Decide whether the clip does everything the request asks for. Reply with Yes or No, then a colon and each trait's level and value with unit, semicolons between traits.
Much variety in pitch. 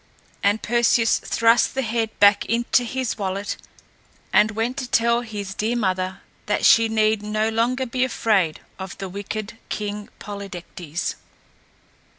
No: narrow, 2.6 semitones